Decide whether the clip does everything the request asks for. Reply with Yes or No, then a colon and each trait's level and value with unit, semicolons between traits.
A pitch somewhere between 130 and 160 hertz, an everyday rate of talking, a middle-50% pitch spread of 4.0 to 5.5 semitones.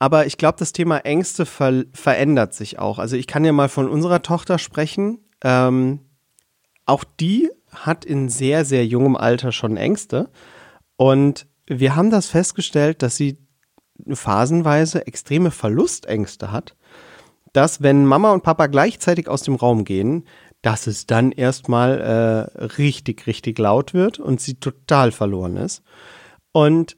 Yes: medium, 140 Hz; average, 145 wpm; average, 4.6 semitones